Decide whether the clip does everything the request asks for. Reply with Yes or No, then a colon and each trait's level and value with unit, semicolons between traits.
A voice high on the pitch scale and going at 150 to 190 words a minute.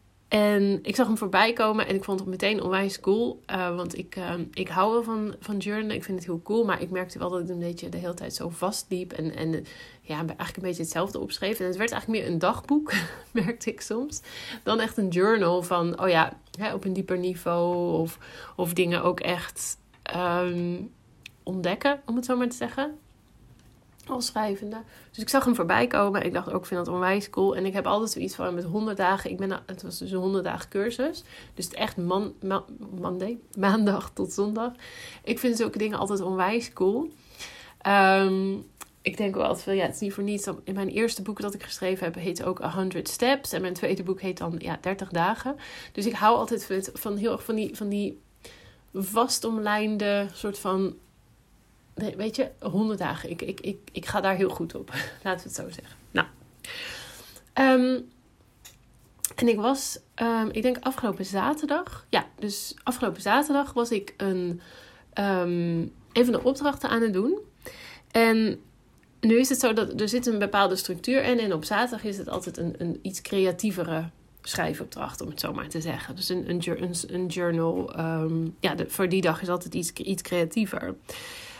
No: high, 195 Hz; fast, 200 wpm